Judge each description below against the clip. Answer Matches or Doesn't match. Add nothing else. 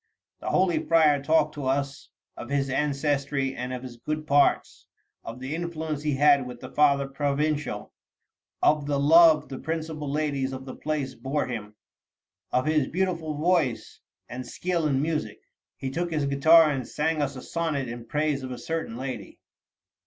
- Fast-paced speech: Doesn't match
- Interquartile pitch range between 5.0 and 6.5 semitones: Doesn't match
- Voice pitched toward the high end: Doesn't match